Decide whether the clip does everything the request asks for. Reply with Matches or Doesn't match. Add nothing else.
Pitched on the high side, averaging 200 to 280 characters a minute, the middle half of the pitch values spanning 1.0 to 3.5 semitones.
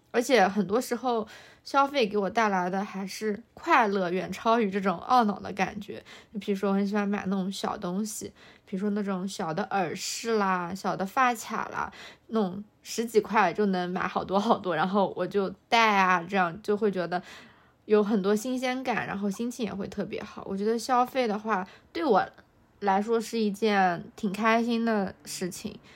Matches